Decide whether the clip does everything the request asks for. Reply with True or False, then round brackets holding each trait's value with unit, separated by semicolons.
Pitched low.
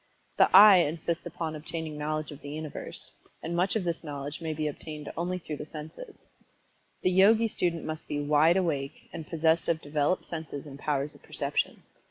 False (155 Hz)